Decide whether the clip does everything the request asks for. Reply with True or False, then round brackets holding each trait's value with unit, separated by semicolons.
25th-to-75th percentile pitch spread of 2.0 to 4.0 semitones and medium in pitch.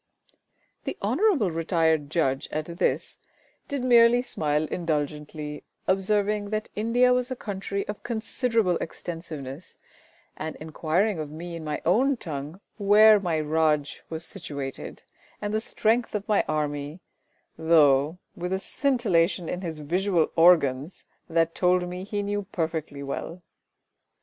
False (5.1 semitones; 175 Hz)